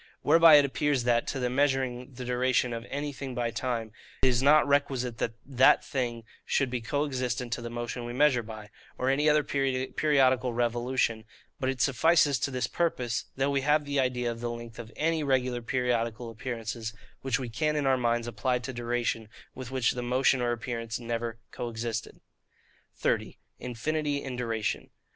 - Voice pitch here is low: Yes, low, 125 Hz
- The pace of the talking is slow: No, average, 180 wpm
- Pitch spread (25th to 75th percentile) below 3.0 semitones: Yes, narrow, 2.5 semitones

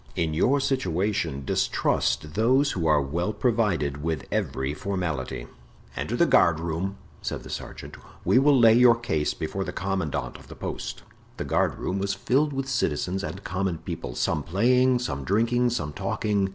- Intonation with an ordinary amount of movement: No, wide, 7.0 semitones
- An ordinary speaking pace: Yes, average, 160 wpm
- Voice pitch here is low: Yes, very low, 95 Hz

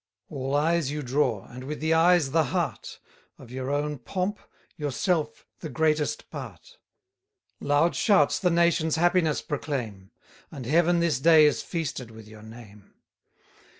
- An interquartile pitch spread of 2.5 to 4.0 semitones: No, average, 4.5 semitones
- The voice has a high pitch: No, medium, 150 Hz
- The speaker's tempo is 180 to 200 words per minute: No, average, 145 wpm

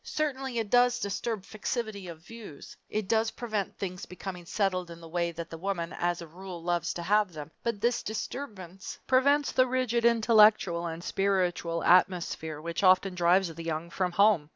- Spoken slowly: No, average, 175 wpm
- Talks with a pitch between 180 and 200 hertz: Yes, high, 190 Hz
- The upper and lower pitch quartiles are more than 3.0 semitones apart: Yes, average, 4.4 semitones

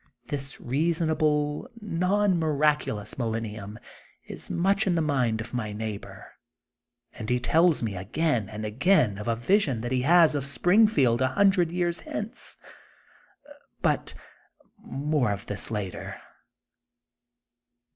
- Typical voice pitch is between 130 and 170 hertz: Yes, medium, 140 Hz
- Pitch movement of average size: No, wide, 7.2 semitones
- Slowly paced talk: Yes, slow, 125 wpm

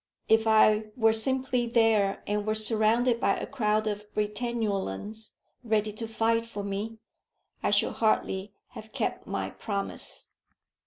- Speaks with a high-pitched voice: Yes, high, 220 Hz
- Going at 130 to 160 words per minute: Yes, average, 140 wpm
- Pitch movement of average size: No, narrow, 1.5 semitones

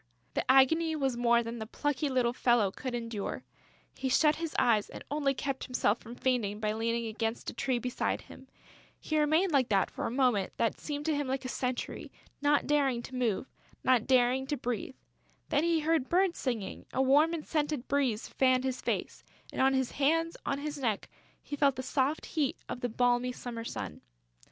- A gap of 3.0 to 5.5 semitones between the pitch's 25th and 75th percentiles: Yes, average, 3.5 semitones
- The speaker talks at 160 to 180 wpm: No, average, 195 wpm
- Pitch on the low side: No, very high, 260 Hz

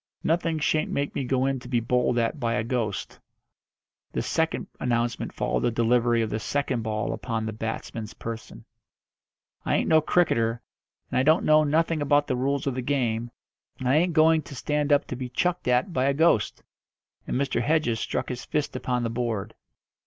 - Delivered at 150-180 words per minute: No, average, 195 wpm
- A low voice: Yes, low, 125 Hz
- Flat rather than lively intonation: No, average, 4.2 semitones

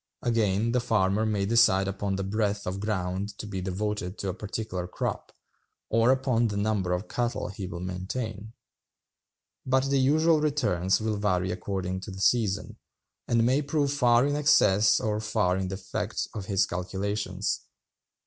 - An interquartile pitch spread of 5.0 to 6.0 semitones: No, average, 3.5 semitones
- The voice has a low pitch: Yes, low, 105 Hz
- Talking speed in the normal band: Yes, average, 160 wpm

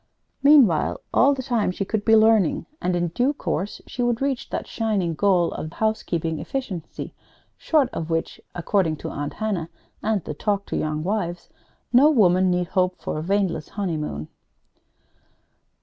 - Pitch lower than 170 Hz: No, high, 190 Hz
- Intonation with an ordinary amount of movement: Yes, average, 4.9 semitones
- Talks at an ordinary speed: Yes, average, 160 wpm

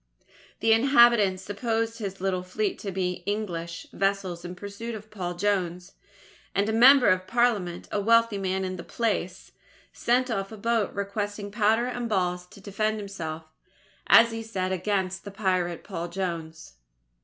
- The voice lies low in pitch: No, high, 200 Hz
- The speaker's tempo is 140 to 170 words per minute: Yes, average, 155 wpm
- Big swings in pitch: No, average, 3.3 semitones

